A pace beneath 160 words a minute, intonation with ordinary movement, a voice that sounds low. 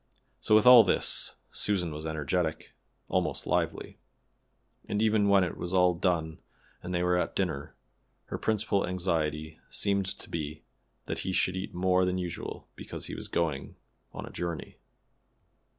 Yes: average, 150 wpm; average, 3.2 semitones; very low, 90 Hz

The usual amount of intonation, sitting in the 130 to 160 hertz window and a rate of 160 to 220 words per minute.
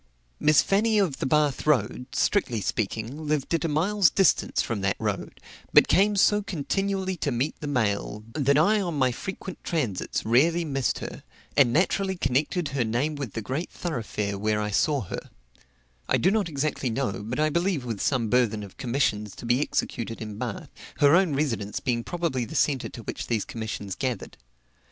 No: wide, 6.5 semitones; medium, 140 Hz; average, 185 wpm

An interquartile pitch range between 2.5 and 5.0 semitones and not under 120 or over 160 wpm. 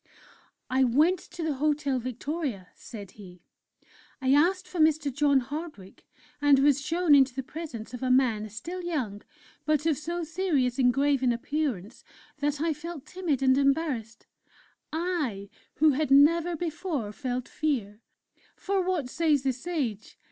Yes: average, 4.4 semitones; average, 150 wpm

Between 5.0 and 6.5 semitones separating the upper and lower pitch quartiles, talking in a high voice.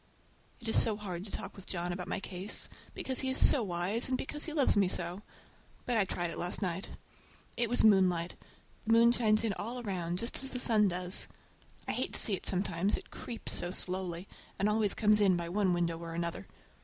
No: average, 4.2 semitones; high, 195 Hz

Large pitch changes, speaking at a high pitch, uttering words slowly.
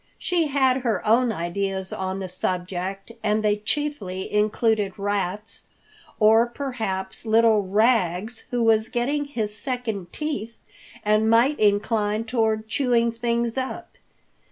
No: average, 3.1 semitones; high, 220 Hz; slow, 125 wpm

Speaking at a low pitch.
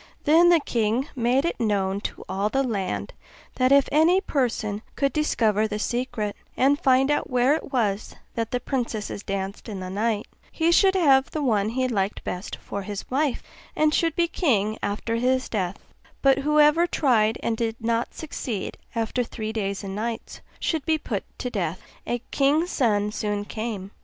No: high, 235 Hz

